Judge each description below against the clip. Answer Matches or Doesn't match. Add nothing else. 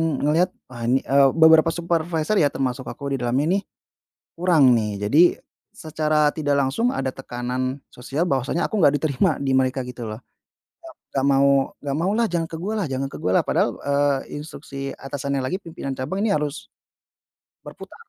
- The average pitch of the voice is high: Doesn't match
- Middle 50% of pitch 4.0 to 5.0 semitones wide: Doesn't match